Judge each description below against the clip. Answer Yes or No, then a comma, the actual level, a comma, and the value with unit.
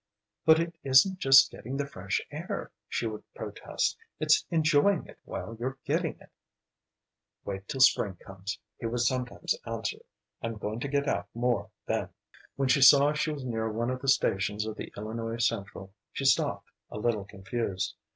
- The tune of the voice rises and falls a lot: No, average, 4.3 semitones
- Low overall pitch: Yes, low, 120 Hz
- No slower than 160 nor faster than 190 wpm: Yes, average, 170 wpm